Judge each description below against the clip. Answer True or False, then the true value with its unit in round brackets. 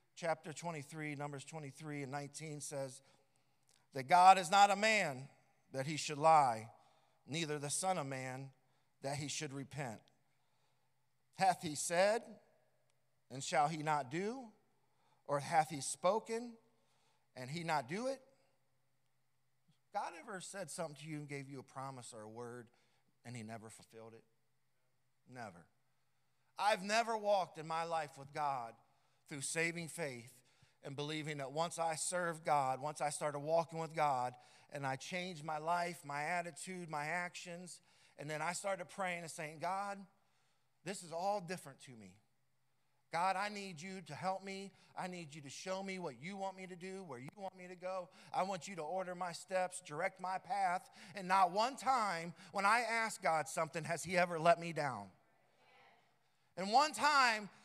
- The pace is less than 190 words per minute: True (170 wpm)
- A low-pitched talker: False (160 Hz)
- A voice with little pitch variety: False (5.2 semitones)